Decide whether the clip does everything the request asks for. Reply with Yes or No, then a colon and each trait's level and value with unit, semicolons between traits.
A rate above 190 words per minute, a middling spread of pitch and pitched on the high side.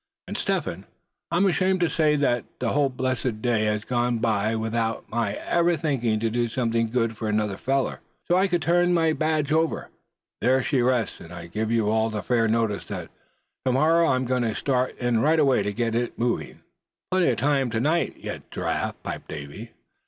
No: average, 200 wpm; average, 4.8 semitones; low, 120 Hz